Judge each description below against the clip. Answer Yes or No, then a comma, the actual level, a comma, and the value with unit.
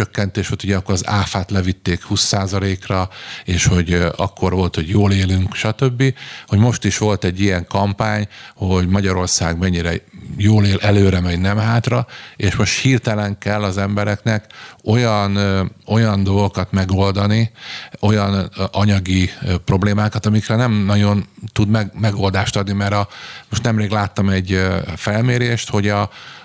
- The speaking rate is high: No, average, 135 wpm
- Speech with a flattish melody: Yes, narrow, 1.9 semitones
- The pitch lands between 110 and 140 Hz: No, low, 100 Hz